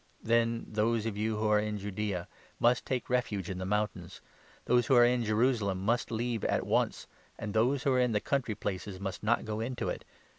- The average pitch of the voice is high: No, low, 110 Hz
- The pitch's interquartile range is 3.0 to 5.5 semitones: No, narrow, 2.6 semitones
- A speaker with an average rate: No, fast, 215 wpm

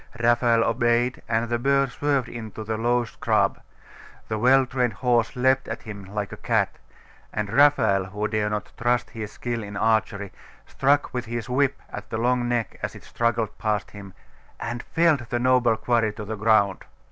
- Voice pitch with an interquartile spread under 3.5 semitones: Yes, narrow, 2.4 semitones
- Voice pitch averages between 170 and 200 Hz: No, low, 115 Hz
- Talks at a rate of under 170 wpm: No, average, 180 wpm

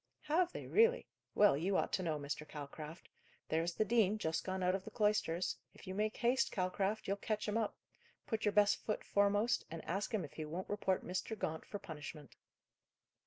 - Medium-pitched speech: No, high, 195 Hz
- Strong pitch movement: No, average, 4.5 semitones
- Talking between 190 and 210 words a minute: Yes, average, 200 wpm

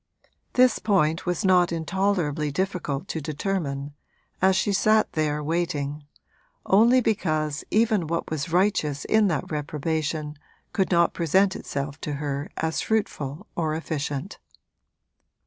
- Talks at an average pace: No, slow, 125 wpm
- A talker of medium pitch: Yes, medium, 160 Hz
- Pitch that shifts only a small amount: No, average, 4.4 semitones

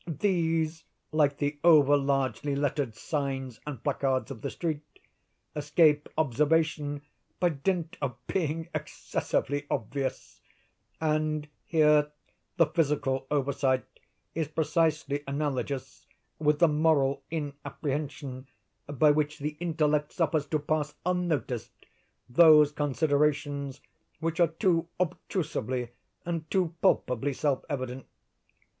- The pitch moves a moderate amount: No, narrow, 2.3 semitones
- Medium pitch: Yes, medium, 150 Hz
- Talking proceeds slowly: Yes, slow, 105 wpm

